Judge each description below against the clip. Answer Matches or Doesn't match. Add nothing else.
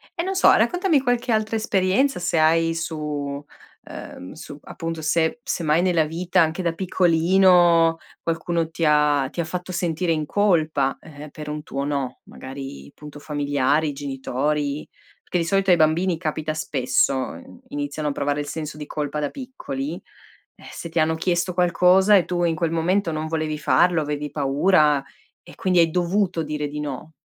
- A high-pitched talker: Doesn't match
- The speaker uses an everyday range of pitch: Matches